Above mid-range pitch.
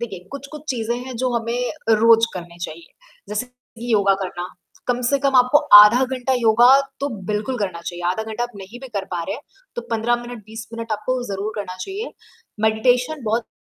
Yes: high, 230 Hz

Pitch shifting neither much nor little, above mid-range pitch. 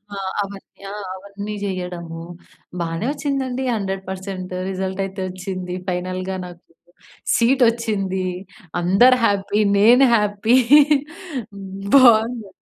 Yes: average, 3.5 semitones; high, 195 Hz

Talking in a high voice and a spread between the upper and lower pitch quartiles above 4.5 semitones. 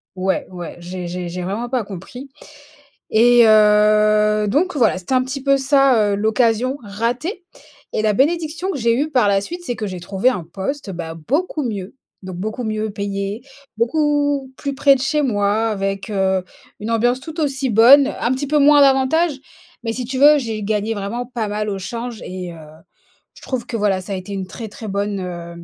Yes: high, 225 Hz; average, 5.1 semitones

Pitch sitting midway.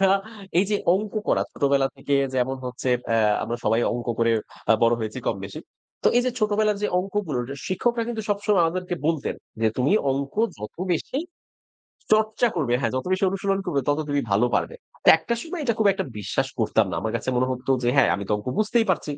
Yes: medium, 145 Hz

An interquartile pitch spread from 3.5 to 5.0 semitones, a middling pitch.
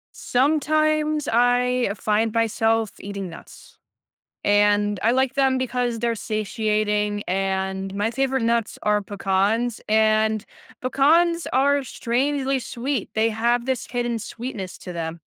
No: average, 3.8 semitones; high, 230 Hz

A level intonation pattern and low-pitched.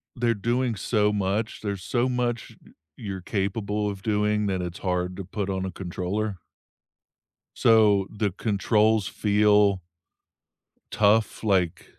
Yes: narrow, 2.2 semitones; low, 105 Hz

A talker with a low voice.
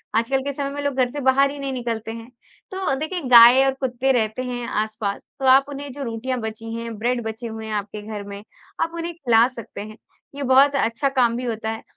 No: high, 245 Hz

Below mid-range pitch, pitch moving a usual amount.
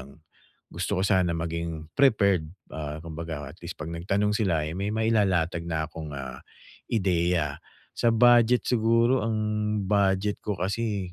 Yes: very low, 90 Hz; average, 4.4 semitones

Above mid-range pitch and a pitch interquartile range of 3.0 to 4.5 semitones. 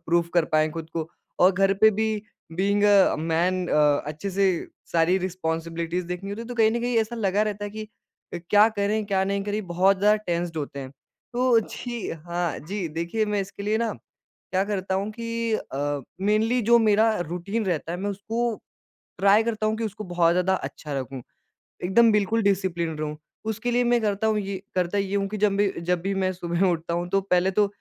Yes: high, 195 Hz; average, 3.8 semitones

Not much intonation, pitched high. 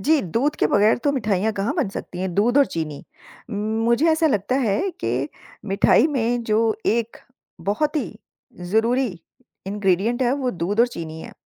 No: average, 4.8 semitones; high, 225 Hz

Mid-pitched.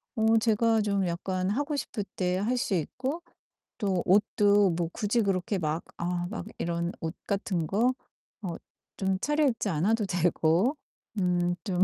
No: high, 195 Hz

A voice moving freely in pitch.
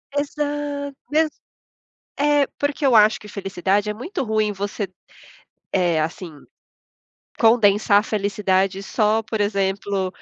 Yes: wide, 5.8 semitones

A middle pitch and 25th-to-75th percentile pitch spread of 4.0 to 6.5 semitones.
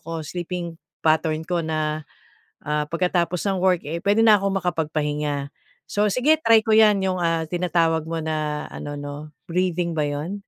No: medium, 165 Hz; average, 3.2 semitones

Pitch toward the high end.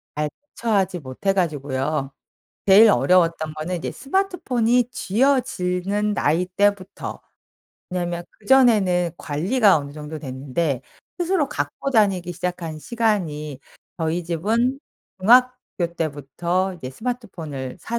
No: medium, 180 Hz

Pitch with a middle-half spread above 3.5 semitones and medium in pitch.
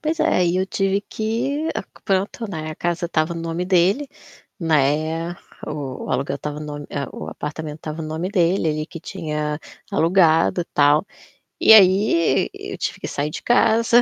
Yes: average, 4.1 semitones; medium, 165 Hz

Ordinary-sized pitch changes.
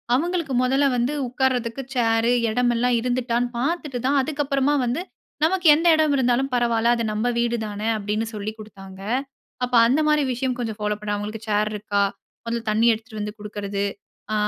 Yes: average, 3.7 semitones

